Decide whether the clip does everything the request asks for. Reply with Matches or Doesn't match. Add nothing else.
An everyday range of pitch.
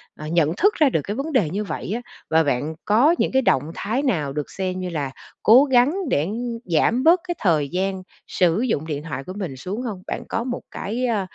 Doesn't match